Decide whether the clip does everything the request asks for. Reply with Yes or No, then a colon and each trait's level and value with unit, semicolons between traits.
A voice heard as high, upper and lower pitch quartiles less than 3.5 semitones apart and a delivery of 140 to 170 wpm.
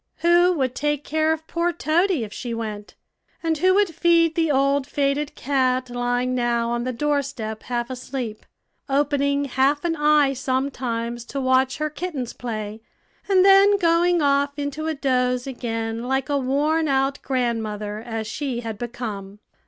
No: very high, 270 Hz; average, 4.0 semitones; average, 160 wpm